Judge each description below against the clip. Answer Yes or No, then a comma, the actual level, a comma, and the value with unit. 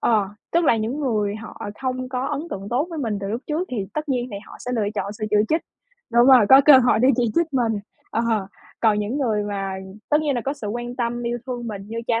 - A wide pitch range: No, average, 3.8 semitones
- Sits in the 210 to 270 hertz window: Yes, high, 240 Hz